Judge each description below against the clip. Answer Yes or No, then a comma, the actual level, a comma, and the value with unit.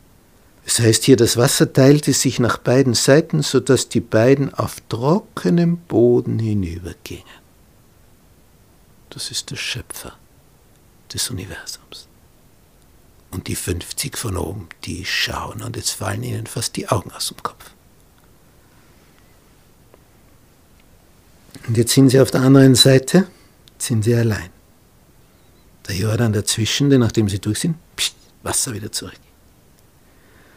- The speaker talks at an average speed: No, slow, 120 wpm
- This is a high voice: No, low, 120 Hz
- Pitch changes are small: No, average, 4.3 semitones